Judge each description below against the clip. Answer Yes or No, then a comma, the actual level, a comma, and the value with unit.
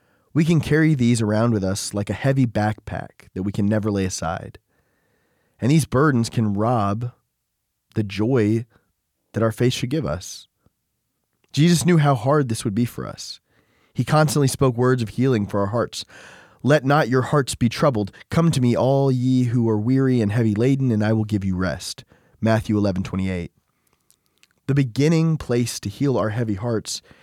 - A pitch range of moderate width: Yes, average, 4.3 semitones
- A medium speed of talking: Yes, average, 185 wpm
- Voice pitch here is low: Yes, low, 120 Hz